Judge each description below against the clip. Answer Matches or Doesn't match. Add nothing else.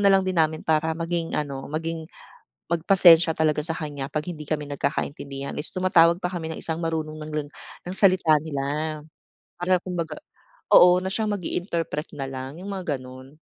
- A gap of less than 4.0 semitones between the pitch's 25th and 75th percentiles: Matches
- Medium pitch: Matches